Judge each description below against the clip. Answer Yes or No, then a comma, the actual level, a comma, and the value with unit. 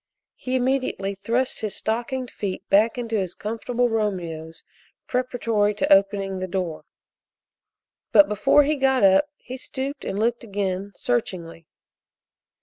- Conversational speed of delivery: No, slow, 130 wpm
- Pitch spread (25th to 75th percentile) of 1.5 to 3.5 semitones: No, average, 4.2 semitones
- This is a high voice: Yes, high, 215 Hz